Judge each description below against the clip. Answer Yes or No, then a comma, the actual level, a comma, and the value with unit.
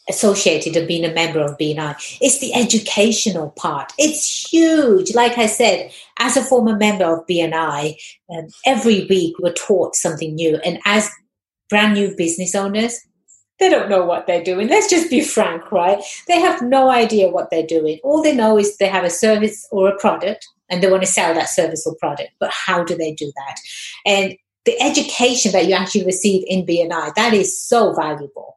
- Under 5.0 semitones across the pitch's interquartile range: No, average, 5.3 semitones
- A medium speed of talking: Yes, average, 195 wpm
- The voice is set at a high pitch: Yes, high, 195 Hz